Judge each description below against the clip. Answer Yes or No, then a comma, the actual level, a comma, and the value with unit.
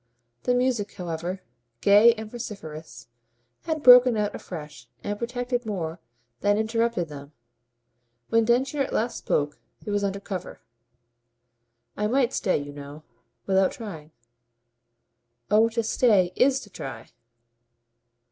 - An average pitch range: No, wide, 5.8 semitones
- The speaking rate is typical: No, slow, 125 wpm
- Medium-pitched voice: No, high, 205 Hz